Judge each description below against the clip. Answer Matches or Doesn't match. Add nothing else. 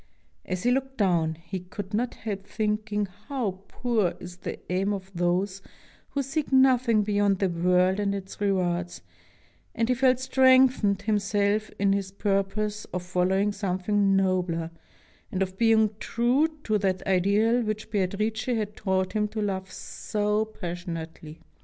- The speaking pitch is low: Doesn't match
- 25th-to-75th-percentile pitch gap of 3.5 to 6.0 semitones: Doesn't match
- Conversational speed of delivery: Matches